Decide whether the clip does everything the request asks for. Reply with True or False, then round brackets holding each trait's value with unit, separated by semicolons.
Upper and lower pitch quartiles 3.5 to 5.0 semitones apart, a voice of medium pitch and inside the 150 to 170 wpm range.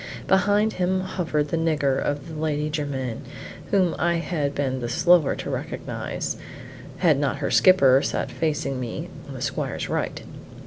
True (4.1 semitones; 150 Hz; 155 wpm)